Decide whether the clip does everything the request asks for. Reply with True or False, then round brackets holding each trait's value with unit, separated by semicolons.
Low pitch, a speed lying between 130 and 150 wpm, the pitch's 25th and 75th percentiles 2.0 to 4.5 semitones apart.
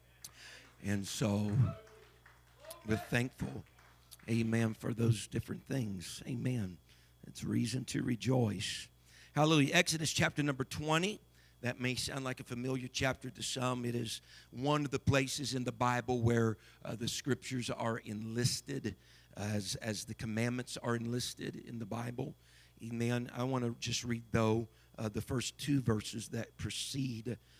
True (120 Hz; 145 wpm; 2.9 semitones)